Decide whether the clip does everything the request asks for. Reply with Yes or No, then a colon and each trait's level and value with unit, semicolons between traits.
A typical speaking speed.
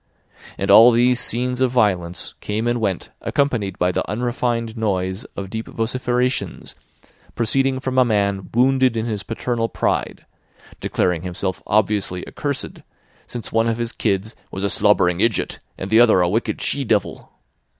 Yes: average, 155 wpm